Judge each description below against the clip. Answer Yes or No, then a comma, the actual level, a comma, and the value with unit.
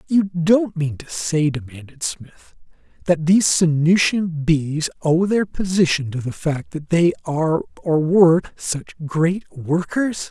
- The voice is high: No, medium, 160 Hz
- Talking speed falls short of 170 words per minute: Yes, average, 145 wpm